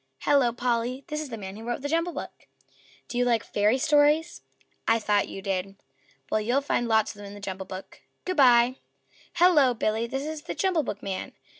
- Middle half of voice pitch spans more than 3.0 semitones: Yes, wide, 5.6 semitones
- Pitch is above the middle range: Yes, high, 240 Hz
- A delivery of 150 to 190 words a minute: No, average, 200 wpm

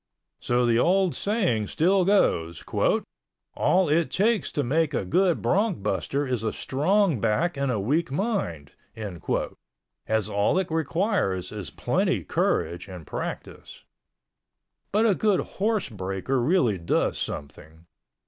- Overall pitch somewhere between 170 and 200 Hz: No, medium, 140 Hz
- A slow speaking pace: Yes, slow, 130 wpm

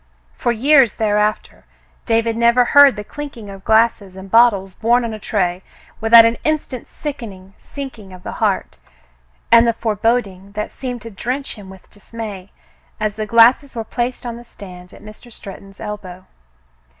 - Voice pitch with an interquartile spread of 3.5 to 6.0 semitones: No, average, 3.1 semitones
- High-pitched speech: Yes, high, 225 Hz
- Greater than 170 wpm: No, average, 160 wpm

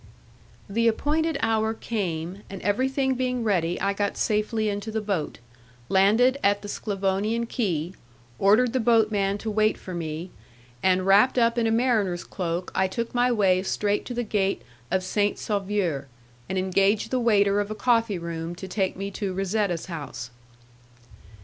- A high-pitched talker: Yes, high, 205 Hz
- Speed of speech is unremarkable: Yes, average, 160 wpm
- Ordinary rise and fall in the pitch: Yes, average, 3.2 semitones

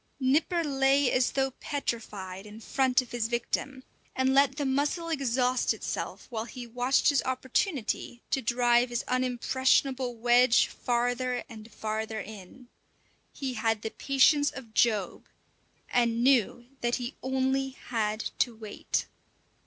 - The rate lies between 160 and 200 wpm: No, slow, 135 wpm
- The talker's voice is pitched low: No, very high, 250 Hz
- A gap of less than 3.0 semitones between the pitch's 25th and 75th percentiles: Yes, narrow, 2.5 semitones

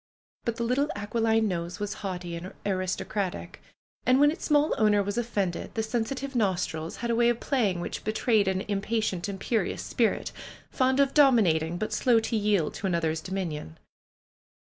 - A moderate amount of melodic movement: Yes, average, 4.2 semitones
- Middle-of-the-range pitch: No, high, 210 Hz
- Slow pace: No, average, 170 wpm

